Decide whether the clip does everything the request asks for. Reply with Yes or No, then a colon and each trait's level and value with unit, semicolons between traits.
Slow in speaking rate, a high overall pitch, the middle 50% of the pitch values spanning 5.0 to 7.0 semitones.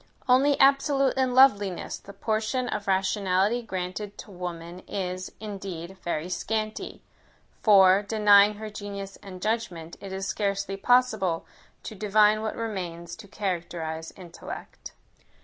No: slow, 125 wpm; high, 200 Hz; average, 2.9 semitones